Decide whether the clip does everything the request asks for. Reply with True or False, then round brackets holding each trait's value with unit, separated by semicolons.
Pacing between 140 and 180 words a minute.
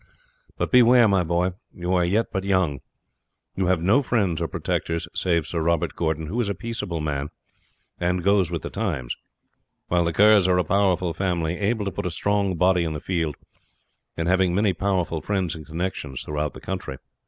False (190 wpm)